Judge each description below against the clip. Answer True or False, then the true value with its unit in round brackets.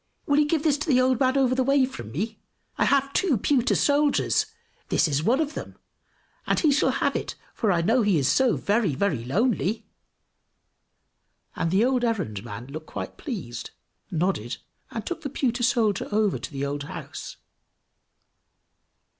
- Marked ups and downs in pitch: True (8.4 semitones)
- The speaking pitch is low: False (230 Hz)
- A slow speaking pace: False (175 wpm)